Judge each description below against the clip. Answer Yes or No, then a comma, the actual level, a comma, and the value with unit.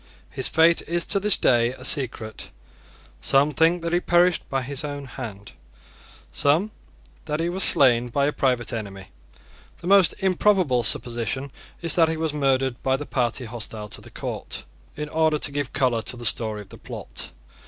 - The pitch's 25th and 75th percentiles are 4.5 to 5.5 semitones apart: Yes, average, 5.2 semitones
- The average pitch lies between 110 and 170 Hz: Yes, medium, 140 Hz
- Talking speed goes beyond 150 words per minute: Yes, average, 180 wpm